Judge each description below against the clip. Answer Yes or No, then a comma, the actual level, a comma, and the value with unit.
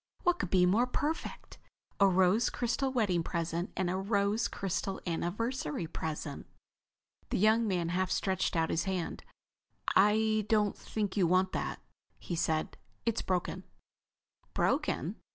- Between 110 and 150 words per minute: Yes, slow, 135 wpm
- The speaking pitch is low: No, high, 190 Hz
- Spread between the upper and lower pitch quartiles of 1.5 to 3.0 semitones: No, average, 3.6 semitones